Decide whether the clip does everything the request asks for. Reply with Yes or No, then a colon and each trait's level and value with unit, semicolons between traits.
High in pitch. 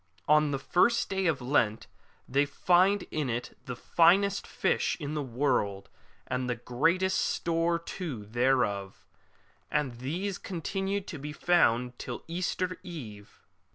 No: medium, 150 Hz